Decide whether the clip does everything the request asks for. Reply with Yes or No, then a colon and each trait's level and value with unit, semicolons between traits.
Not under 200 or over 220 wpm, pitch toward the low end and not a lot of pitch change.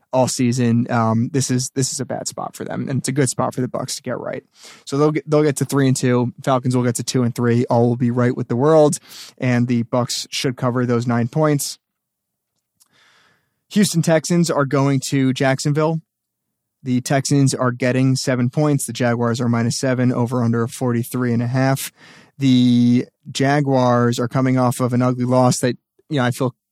Yes: fast, 205 wpm; low, 125 Hz; narrow, 2.2 semitones